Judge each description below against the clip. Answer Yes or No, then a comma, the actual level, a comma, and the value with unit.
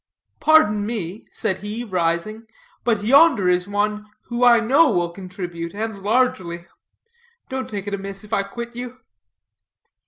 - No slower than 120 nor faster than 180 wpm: Yes, average, 145 wpm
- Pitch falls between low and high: No, high, 210 Hz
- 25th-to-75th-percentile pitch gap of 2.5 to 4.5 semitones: Yes, average, 4.0 semitones